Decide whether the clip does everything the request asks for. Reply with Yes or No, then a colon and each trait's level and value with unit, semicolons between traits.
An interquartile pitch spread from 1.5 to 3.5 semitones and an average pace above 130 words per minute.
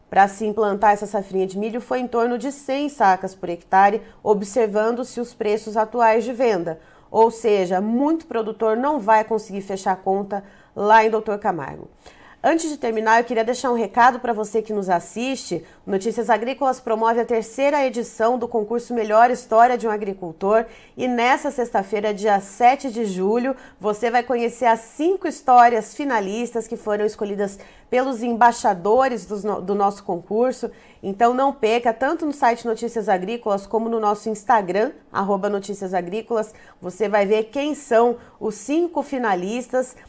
Yes: average, 2.8 semitones; average, 160 wpm